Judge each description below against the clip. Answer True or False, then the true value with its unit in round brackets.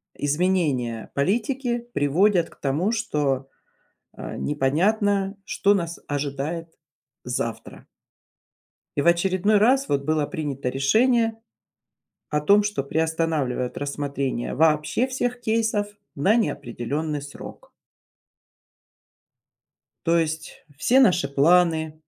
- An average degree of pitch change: False (6.5 semitones)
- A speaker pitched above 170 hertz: False (160 Hz)